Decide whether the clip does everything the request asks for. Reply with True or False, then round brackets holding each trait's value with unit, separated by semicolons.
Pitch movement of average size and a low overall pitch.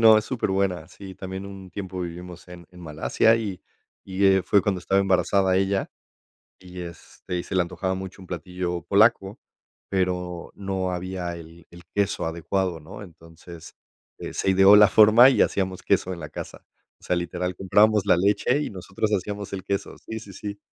False (2.0 semitones; 95 Hz)